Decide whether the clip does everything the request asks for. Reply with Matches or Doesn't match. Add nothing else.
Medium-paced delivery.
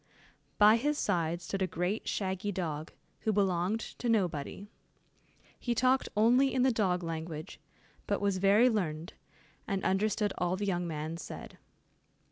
Matches